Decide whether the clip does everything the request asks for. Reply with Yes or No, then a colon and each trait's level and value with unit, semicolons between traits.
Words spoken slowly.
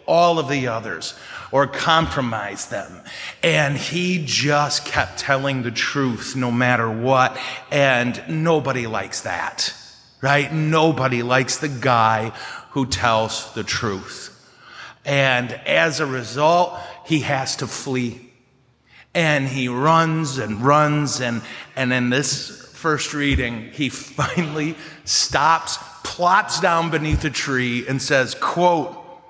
Yes: slow, 125 wpm